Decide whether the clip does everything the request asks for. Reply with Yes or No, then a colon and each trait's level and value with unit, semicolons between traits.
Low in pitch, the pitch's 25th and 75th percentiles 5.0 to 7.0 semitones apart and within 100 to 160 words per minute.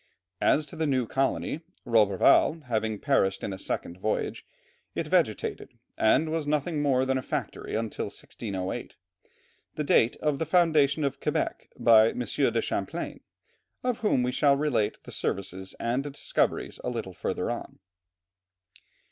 Yes: low, 130 Hz; average, 5.3 semitones; average, 150 wpm